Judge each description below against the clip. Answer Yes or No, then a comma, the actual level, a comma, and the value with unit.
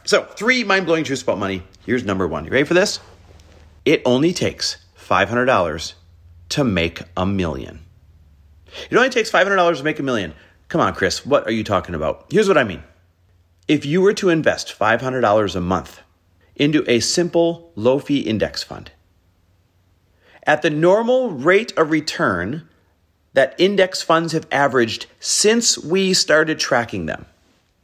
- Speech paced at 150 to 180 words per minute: Yes, average, 155 wpm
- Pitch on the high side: No, low, 110 Hz